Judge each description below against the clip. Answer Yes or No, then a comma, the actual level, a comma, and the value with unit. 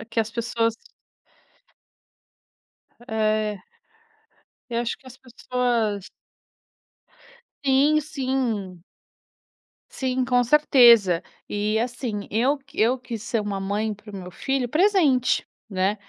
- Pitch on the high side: Yes, high, 235 Hz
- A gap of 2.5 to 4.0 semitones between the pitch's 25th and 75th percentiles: Yes, average, 3.6 semitones